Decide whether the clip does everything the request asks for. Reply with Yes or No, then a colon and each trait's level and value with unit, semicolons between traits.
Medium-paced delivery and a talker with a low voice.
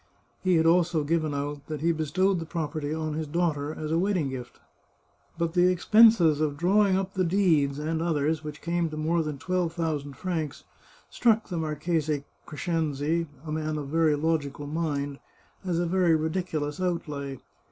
No: average, 175 wpm; medium, 160 Hz